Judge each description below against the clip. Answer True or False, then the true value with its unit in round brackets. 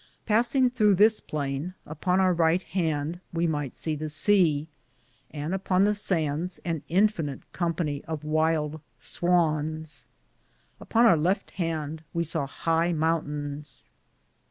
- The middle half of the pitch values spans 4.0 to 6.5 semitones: False (3.3 semitones)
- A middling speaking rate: False (130 wpm)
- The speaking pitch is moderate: True (165 Hz)